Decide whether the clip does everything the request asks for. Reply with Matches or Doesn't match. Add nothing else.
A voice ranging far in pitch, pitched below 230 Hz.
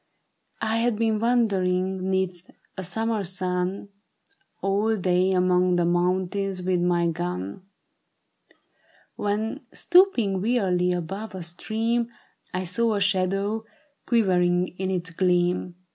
Doesn't match